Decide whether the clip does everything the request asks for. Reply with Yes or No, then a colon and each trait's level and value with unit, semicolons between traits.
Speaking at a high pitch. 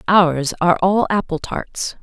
No: medium, 180 Hz